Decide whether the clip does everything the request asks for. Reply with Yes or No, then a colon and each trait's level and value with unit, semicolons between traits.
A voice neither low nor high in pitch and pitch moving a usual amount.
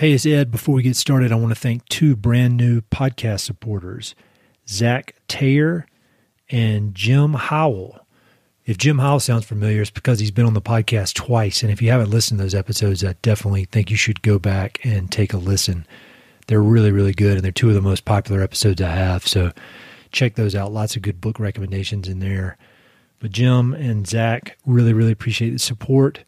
No: low, 110 Hz; average, 3.4 semitones